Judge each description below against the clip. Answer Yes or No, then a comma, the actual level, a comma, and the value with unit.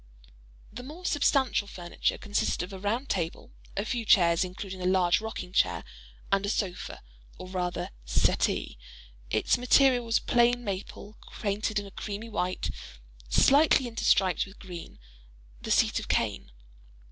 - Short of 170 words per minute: Yes, average, 140 wpm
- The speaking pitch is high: Yes, high, 200 Hz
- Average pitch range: Yes, average, 4.3 semitones